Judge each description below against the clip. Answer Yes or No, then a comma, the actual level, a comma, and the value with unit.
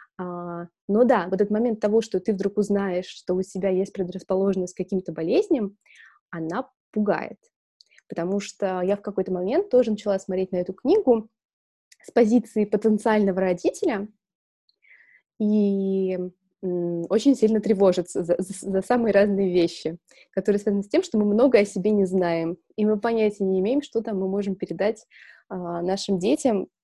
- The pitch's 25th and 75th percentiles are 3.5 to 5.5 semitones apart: No, average, 2.8 semitones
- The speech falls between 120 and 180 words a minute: Yes, average, 155 wpm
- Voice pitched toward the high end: Yes, high, 195 Hz